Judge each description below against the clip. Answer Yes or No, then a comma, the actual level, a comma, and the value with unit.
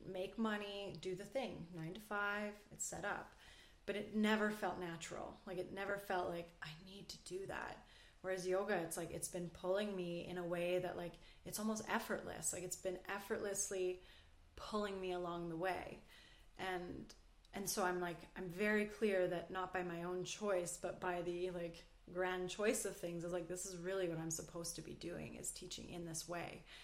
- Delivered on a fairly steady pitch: Yes, narrow, 2.3 semitones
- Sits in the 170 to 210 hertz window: Yes, medium, 185 Hz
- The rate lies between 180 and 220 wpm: Yes, average, 200 wpm